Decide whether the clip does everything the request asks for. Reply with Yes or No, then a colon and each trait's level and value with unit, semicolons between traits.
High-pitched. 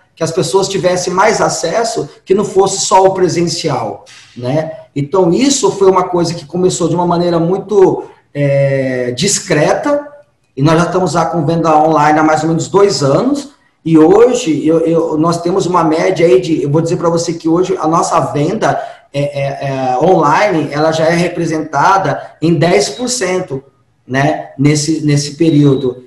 No: medium, 165 Hz